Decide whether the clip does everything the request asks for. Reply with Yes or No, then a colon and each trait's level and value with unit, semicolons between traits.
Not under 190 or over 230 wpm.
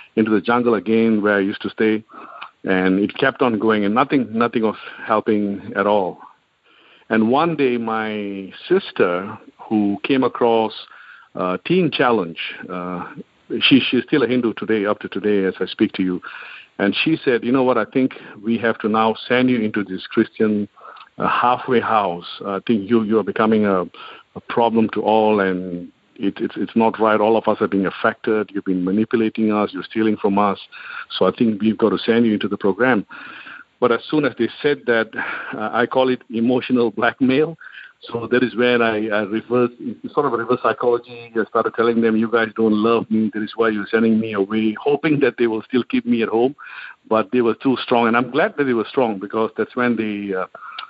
Yes: fast, 205 wpm